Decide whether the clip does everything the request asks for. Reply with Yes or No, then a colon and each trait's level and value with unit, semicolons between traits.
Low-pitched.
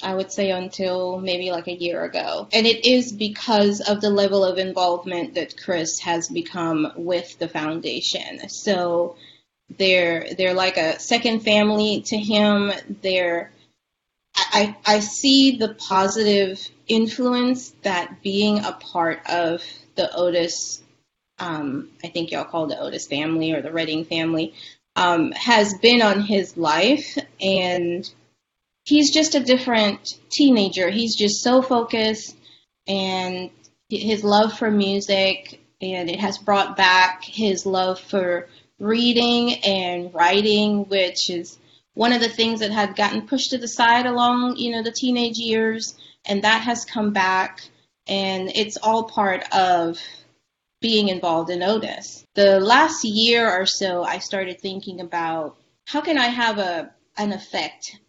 No: high, 200 Hz